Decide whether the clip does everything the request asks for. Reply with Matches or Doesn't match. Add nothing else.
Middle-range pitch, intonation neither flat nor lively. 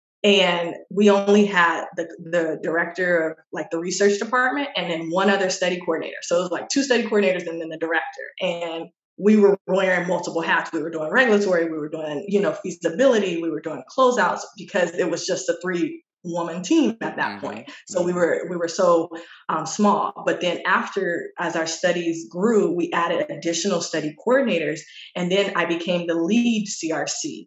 Matches